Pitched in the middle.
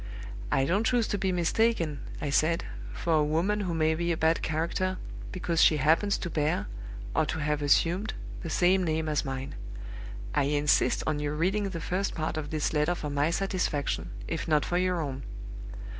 Yes: medium, 160 Hz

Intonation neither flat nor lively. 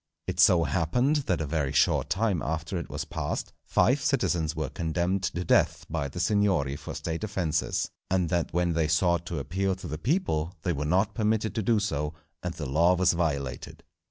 Yes: average, 3.5 semitones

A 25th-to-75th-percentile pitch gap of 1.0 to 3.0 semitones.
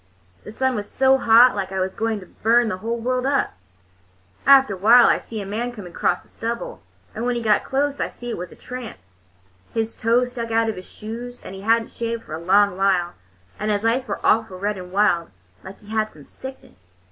No: average, 3.7 semitones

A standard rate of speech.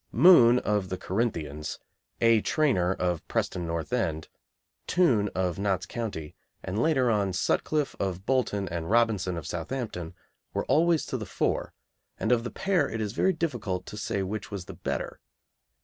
Yes: average, 165 wpm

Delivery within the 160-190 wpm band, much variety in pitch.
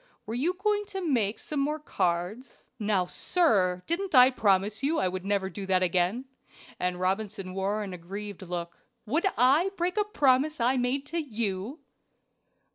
Yes: average, 165 wpm; wide, 7.7 semitones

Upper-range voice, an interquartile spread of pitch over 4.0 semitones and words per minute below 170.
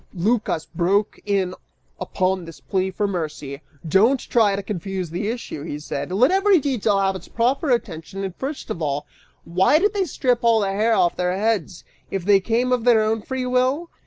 No: high, 205 Hz; average, 5.1 semitones; average, 190 wpm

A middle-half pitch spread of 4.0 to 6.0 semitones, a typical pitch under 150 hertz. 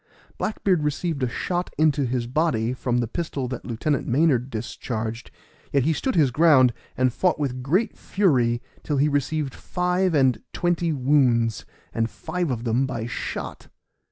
Yes: average, 4.7 semitones; low, 135 Hz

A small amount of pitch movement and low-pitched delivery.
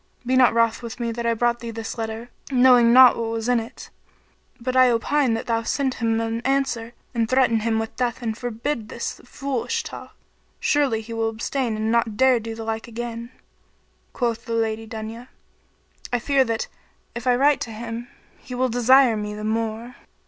No: narrow, 1.7 semitones; high, 235 Hz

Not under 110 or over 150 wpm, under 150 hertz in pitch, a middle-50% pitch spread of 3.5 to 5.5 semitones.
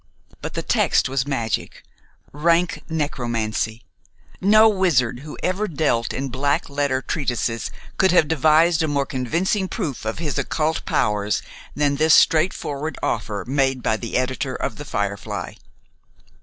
Yes: average, 140 wpm; medium, 140 Hz; average, 4.9 semitones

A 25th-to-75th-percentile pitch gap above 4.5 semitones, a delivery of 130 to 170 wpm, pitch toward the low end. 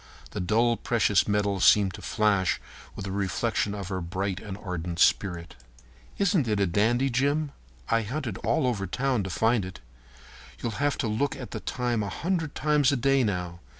No: average, 5.1 semitones; average, 185 wpm; low, 110 Hz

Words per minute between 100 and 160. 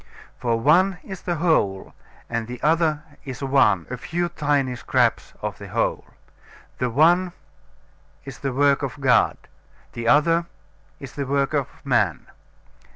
Yes: average, 145 wpm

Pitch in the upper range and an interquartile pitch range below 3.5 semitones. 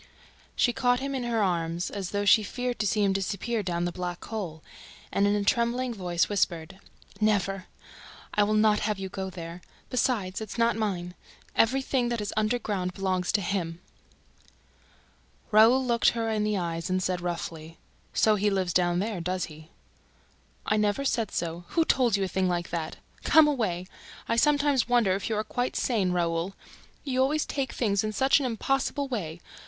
No: high, 205 Hz; average, 4.7 semitones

